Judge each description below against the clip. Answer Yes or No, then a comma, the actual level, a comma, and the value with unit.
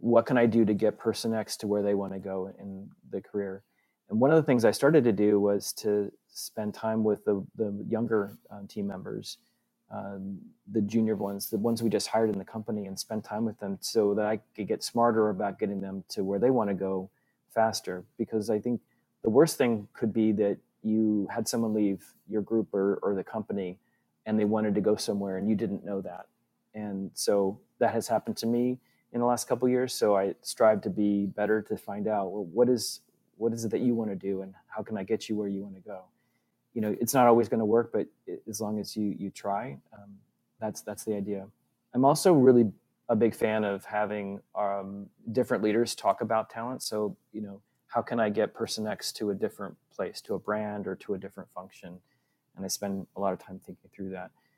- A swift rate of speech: Yes, fast, 230 wpm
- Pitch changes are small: Yes, narrow, 2.2 semitones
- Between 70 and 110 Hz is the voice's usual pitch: Yes, low, 105 Hz